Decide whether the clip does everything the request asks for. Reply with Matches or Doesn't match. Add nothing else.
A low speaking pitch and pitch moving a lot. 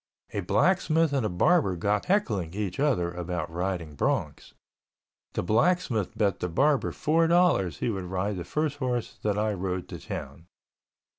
Matches